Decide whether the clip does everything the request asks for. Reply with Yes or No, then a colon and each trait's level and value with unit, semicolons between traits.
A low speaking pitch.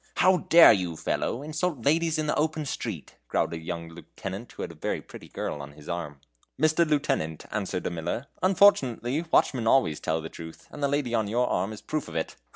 Yes: low, 120 Hz